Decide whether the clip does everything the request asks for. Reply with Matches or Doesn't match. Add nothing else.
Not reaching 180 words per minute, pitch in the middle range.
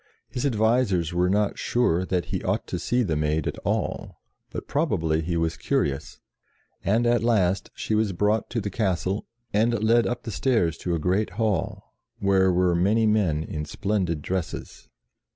Doesn't match